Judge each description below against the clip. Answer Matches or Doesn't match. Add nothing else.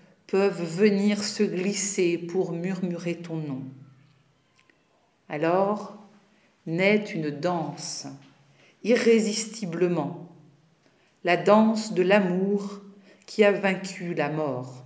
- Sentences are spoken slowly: Matches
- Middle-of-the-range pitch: Matches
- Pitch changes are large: Doesn't match